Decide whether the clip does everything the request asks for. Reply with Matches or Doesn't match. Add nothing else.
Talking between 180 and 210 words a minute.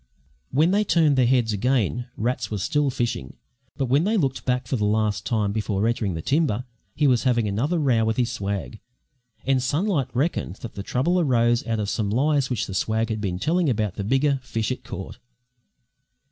Matches